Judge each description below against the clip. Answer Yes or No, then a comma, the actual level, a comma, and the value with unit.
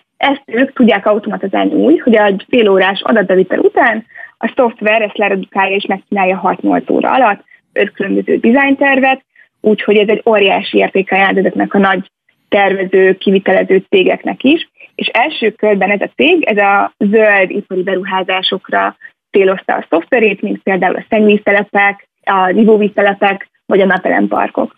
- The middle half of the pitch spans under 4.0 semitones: Yes, average, 2.7 semitones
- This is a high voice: Yes, high, 205 Hz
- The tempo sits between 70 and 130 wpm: No, average, 140 wpm